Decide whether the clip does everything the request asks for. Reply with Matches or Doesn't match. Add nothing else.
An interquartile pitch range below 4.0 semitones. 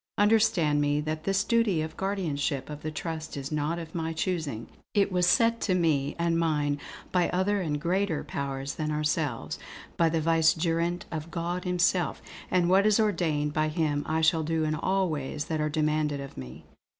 Matches